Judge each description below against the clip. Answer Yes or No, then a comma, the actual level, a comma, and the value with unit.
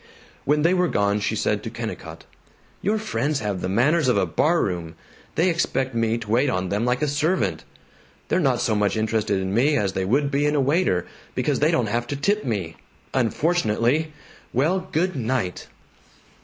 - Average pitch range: No, wide, 6.7 semitones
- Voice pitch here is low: Yes, low, 125 Hz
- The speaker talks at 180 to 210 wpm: Yes, average, 185 wpm